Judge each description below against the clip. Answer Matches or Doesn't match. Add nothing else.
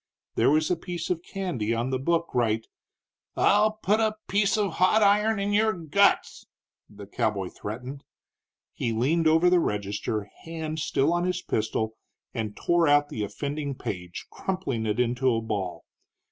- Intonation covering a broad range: Matches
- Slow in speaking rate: Doesn't match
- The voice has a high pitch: Doesn't match